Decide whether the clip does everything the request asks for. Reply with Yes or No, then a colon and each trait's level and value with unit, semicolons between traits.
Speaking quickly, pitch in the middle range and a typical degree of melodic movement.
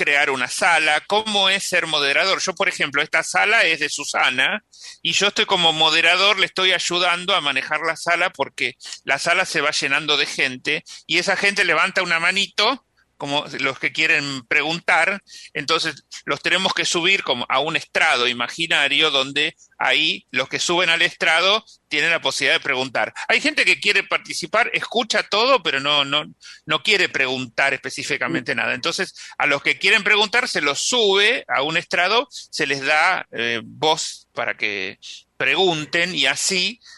No: average, 170 wpm; medium, 160 Hz; average, 4.8 semitones